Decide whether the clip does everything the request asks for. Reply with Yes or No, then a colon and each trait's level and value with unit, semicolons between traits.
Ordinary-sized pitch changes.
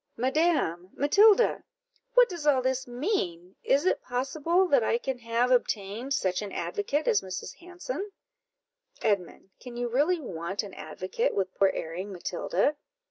No: wide, 8.3 semitones